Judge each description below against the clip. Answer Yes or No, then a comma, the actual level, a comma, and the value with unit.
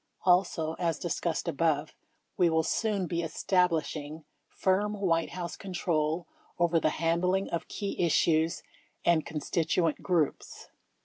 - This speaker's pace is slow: Yes, slow, 125 wpm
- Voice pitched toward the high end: No, medium, 170 Hz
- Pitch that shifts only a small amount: Yes, narrow, 2.1 semitones